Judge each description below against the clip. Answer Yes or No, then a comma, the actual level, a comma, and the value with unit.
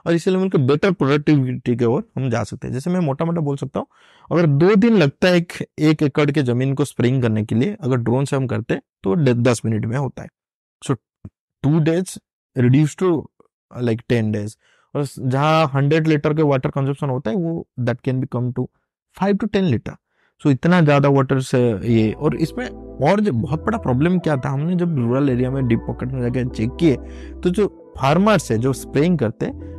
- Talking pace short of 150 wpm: No, average, 200 wpm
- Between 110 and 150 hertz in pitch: Yes, medium, 140 Hz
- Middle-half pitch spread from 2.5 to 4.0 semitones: No, average, 4.8 semitones